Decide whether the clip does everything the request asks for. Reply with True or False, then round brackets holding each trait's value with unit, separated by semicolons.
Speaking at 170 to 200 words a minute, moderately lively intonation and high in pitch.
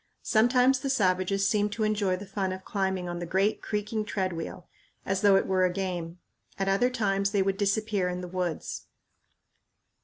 False (180 wpm; 2.3 semitones; 195 Hz)